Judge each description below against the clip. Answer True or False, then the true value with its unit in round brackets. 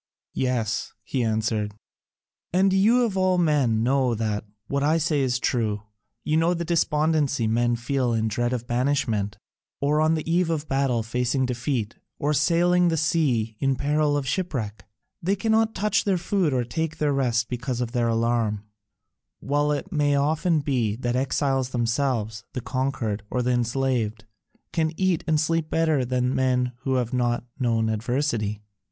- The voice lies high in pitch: False (130 Hz)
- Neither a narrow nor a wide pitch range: True (4.8 semitones)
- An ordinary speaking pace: True (165 wpm)